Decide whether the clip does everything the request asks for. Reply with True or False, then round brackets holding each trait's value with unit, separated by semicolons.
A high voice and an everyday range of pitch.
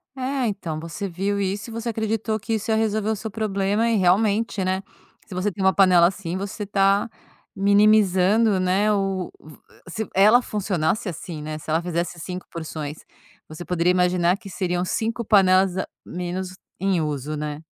True (195 Hz; 3.1 semitones)